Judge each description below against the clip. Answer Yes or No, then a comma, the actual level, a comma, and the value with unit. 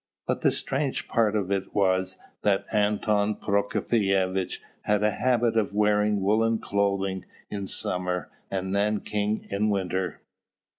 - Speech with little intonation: Yes, narrow, 1.8 semitones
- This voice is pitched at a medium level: No, low, 100 Hz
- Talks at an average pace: No, slow, 130 wpm